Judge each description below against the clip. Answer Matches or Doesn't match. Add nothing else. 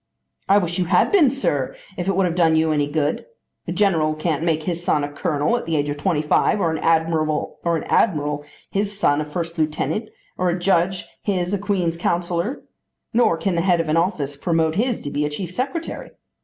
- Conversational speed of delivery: Doesn't match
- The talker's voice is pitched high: Doesn't match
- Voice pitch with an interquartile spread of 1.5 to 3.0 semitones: Doesn't match